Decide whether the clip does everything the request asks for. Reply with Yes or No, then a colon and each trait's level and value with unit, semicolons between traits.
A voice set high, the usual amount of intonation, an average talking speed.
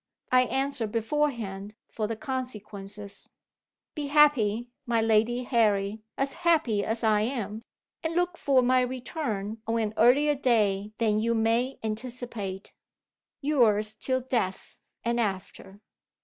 No: high, 230 Hz; average, 3.5 semitones; slow, 125 wpm